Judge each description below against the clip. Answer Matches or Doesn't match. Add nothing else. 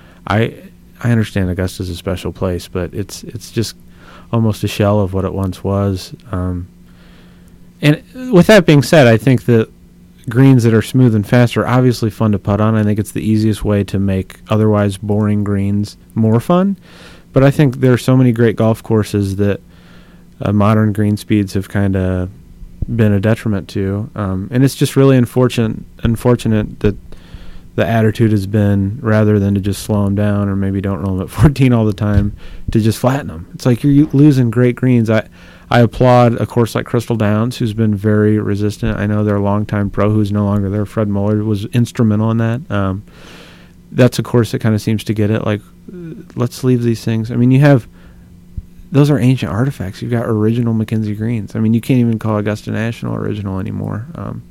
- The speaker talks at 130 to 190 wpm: Doesn't match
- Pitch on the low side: Matches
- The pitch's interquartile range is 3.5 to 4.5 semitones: Doesn't match